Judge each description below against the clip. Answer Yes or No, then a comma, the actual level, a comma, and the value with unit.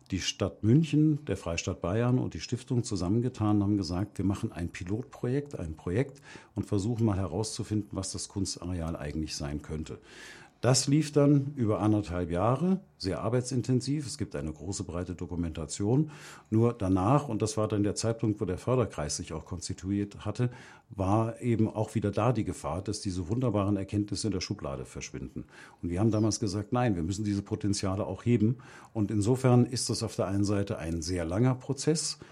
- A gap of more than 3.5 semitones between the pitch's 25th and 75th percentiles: Yes, average, 4.7 semitones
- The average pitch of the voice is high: No, low, 105 Hz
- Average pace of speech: Yes, average, 180 wpm